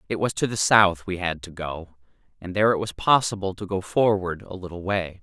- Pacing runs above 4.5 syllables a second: Yes, 5.4 syllables/s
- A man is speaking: Yes, male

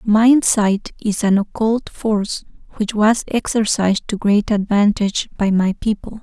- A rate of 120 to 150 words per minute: Yes, average, 145 wpm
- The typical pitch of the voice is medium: No, high, 210 Hz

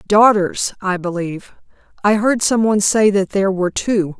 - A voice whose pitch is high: Yes, high, 200 Hz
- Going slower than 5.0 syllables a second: No, 5.2 syllables/s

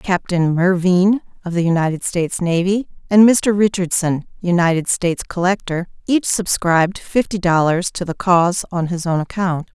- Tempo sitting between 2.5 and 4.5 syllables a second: No, 4.9 syllables/s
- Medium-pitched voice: Yes, medium, 180 Hz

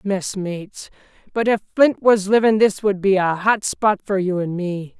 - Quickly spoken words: No, average, 190 wpm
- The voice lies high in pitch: Yes, high, 200 Hz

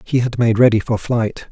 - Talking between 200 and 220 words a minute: No, fast, 240 wpm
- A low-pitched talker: Yes, low, 115 Hz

